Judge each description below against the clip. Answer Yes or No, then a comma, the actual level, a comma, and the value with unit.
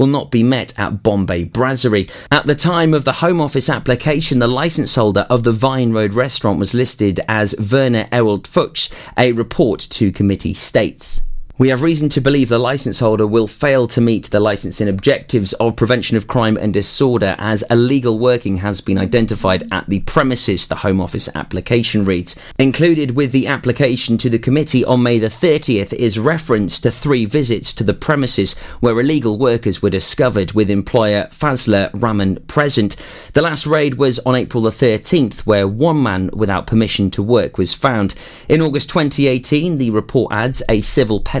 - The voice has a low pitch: Yes, low, 120 Hz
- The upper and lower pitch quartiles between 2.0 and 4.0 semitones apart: No, average, 4.6 semitones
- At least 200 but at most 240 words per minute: No, average, 180 wpm